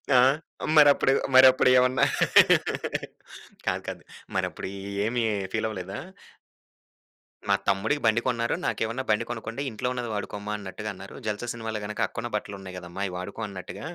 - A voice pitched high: No, low, 110 Hz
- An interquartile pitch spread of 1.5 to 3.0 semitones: No, average, 3.5 semitones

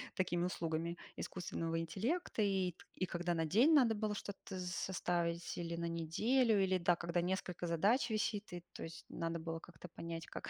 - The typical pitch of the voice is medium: Yes, medium, 175 Hz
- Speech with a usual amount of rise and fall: Yes, average, 3.1 semitones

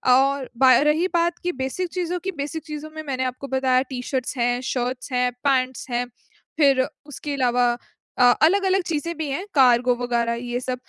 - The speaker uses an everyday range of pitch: Yes, average, 3.8 semitones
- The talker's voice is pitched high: Yes, very high, 265 Hz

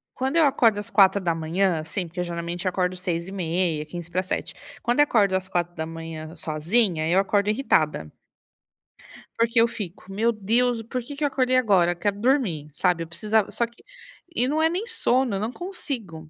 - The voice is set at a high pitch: Yes, high, 195 Hz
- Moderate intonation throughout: No, wide, 5.8 semitones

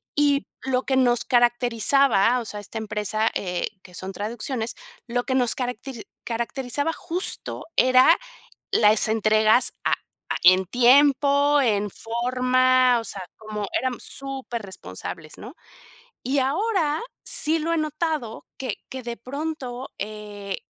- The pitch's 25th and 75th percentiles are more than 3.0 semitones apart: Yes, average, 4.0 semitones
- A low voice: No, high, 245 Hz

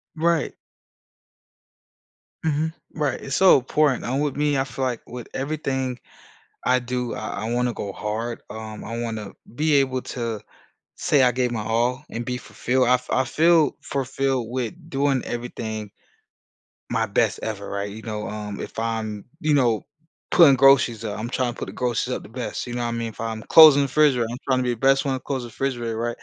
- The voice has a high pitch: No, low, 125 Hz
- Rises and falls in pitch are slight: No, average, 3.2 semitones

